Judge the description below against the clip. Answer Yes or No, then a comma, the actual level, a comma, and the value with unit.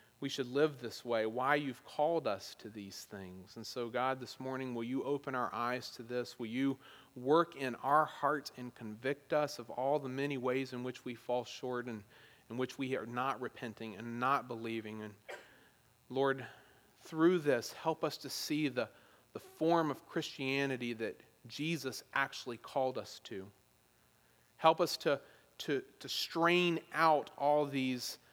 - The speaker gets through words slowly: No, average, 170 wpm